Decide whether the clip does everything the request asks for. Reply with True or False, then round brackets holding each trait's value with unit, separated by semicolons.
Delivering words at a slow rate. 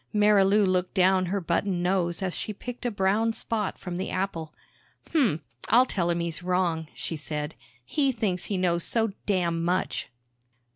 False (165 wpm)